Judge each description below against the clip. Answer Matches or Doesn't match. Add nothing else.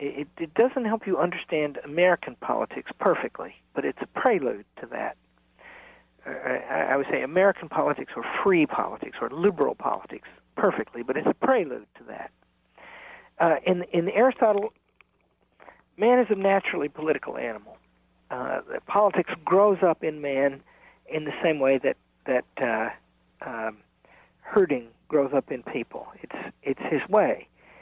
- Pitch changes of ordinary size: Doesn't match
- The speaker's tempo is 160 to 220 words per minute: Doesn't match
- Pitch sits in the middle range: Matches